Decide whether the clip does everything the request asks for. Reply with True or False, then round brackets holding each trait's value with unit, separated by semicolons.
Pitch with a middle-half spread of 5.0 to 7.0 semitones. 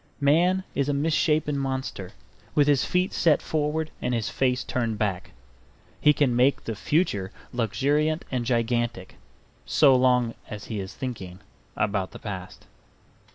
True (5.3 semitones)